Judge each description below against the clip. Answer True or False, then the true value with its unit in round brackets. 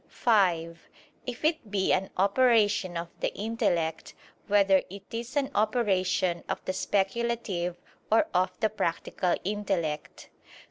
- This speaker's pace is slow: True (125 wpm)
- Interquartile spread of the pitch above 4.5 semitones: False (3.9 semitones)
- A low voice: False (200 Hz)